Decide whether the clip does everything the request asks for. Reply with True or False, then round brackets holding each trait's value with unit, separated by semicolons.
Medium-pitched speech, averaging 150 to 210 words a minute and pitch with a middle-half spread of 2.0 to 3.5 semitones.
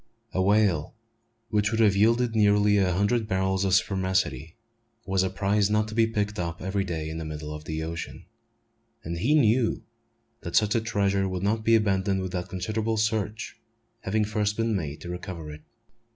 False (100 Hz; 180 wpm; 3.0 semitones)